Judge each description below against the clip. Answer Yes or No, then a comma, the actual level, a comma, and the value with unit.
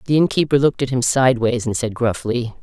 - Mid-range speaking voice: No, low, 125 Hz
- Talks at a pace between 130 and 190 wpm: No, fast, 205 wpm